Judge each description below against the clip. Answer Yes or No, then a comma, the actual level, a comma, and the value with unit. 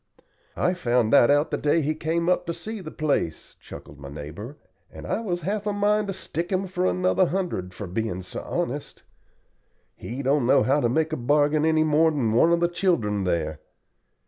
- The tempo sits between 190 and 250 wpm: Yes, average, 200 wpm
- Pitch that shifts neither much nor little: No, wide, 7.2 semitones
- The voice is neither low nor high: Yes, medium, 155 Hz